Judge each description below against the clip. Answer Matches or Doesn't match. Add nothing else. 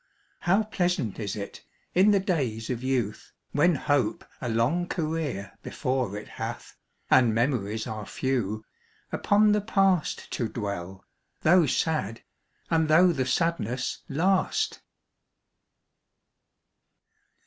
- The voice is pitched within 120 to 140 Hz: Matches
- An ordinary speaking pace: Doesn't match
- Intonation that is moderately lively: Doesn't match